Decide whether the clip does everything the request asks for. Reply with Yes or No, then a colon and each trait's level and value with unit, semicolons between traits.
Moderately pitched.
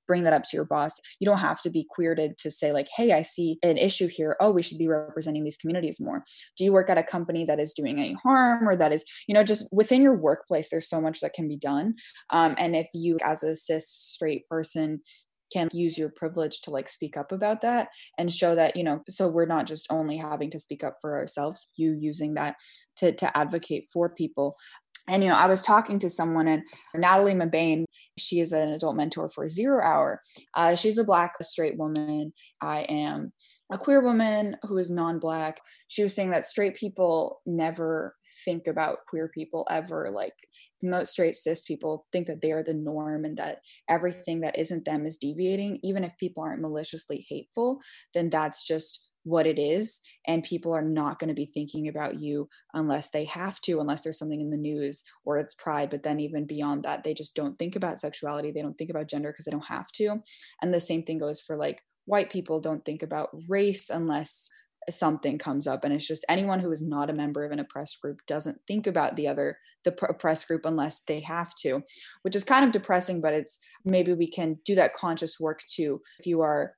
Yes: medium, 160 Hz